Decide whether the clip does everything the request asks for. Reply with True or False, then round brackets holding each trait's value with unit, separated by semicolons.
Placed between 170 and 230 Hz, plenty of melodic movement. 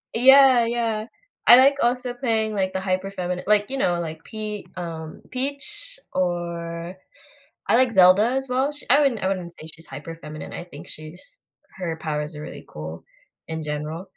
True (190 Hz; 6.7 semitones)